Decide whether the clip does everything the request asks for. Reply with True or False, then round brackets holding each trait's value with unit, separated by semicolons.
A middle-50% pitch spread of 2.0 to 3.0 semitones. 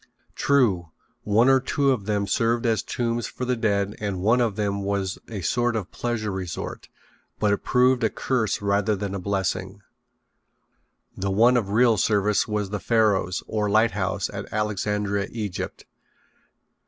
True (2.7 semitones)